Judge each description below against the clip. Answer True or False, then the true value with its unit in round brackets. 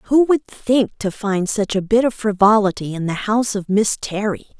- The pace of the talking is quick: True (210 wpm)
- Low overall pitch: False (210 Hz)